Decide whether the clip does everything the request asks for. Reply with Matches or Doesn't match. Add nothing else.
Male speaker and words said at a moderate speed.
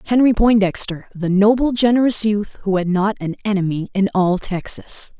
Doesn't match